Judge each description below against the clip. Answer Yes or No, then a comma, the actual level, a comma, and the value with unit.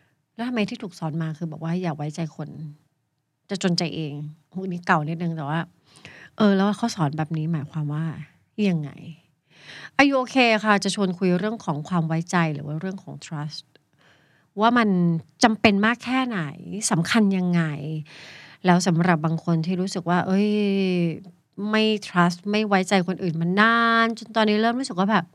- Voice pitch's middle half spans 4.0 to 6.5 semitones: Yes, average, 4.5 semitones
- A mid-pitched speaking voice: Yes, medium, 175 Hz